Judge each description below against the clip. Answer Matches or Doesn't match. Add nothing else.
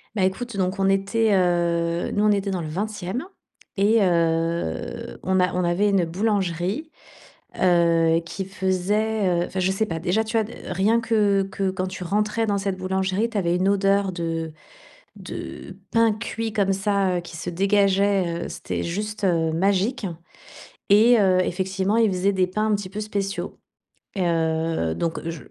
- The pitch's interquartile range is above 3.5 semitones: Doesn't match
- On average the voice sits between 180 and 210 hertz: Matches